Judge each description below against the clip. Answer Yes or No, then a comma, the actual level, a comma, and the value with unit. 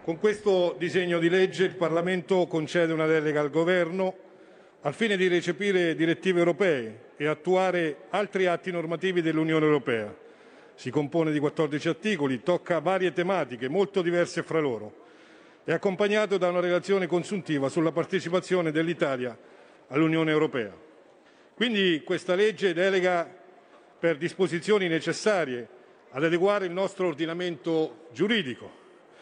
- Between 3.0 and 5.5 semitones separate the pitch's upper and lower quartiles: No, narrow, 2.6 semitones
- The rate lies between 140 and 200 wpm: No, average, 125 wpm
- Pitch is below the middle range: No, medium, 175 Hz